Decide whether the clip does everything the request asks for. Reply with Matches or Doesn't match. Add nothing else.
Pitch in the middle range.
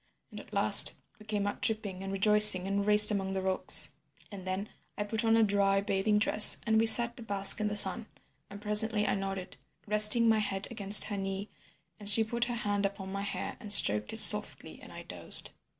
Doesn't match